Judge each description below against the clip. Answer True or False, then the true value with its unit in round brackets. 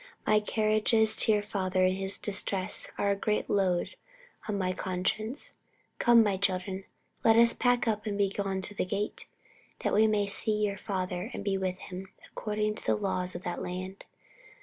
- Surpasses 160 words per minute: True (185 wpm)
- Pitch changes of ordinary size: False (2.2 semitones)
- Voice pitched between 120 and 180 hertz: False (200 Hz)